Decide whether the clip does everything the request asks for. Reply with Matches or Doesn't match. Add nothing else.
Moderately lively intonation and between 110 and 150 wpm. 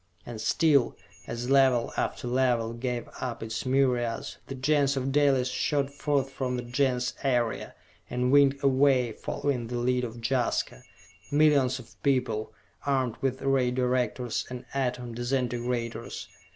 Doesn't match